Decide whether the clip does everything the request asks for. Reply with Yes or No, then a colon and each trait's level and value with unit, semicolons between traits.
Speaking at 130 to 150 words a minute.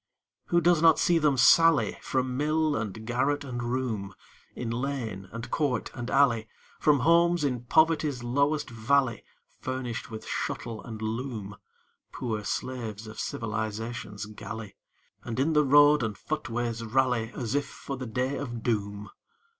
Yes: average, 145 wpm